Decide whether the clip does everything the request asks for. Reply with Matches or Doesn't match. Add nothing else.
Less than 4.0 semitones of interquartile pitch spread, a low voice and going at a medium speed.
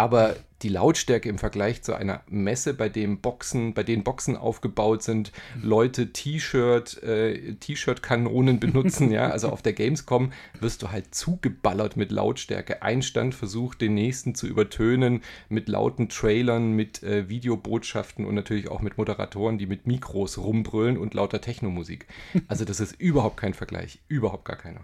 Matches